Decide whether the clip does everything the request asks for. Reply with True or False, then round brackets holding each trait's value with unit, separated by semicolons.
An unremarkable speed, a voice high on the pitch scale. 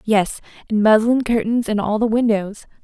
True (170 wpm; 215 Hz)